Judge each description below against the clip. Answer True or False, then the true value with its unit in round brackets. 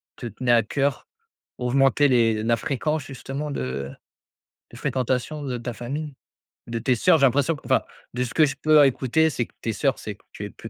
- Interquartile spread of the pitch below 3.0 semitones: False (3.4 semitones)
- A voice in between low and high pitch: False (130 Hz)